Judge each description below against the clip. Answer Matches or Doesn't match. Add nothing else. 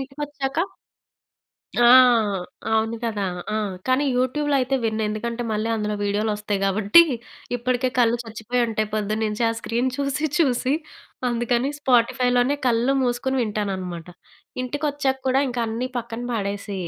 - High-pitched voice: Matches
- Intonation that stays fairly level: Doesn't match